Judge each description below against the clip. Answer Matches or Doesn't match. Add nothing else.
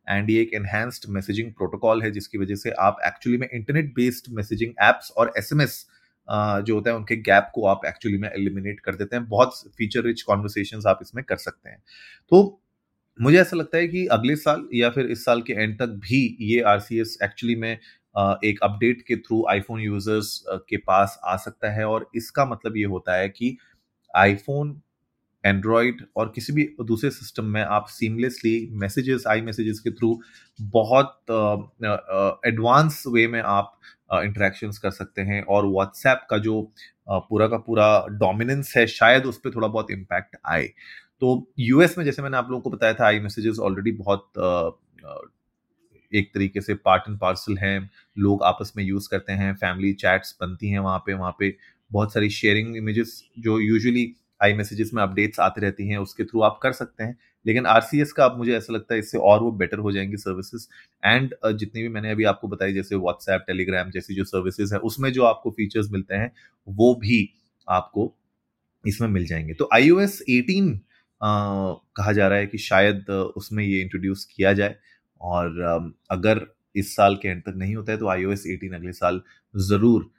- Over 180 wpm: Matches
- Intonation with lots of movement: Doesn't match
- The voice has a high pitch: Doesn't match